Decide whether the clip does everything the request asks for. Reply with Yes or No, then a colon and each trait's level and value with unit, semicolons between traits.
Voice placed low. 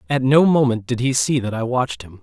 Yes: low, 125 Hz